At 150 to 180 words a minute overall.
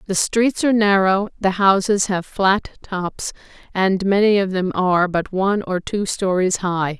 Yes: average, 170 wpm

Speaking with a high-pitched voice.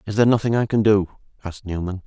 No: low, 100 Hz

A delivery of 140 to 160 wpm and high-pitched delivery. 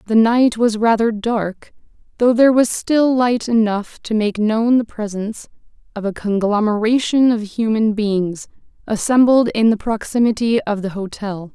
Yes: average, 150 wpm; high, 220 Hz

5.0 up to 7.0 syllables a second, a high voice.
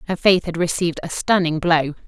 No: 5.7 syllables/s; medium, 170 Hz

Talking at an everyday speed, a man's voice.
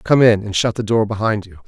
No: fast, 285 wpm; male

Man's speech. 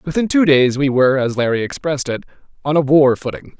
Yes: male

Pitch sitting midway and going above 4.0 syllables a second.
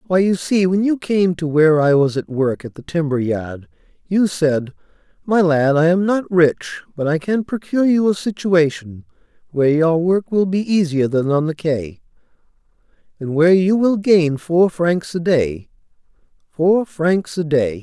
Yes: medium, 170 Hz; 4.5 syllables/s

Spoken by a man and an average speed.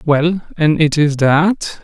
Yes: male; average, 165 wpm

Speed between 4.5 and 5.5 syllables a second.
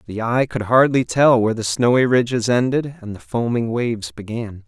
Yes: 5.1 syllables/s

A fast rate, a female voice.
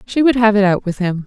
Yes: fast, 330 wpm; female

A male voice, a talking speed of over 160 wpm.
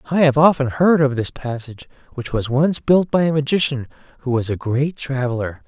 Yes: male; average, 200 wpm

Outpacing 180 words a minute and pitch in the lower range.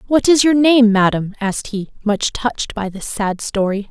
No: average, 200 wpm; high, 220 Hz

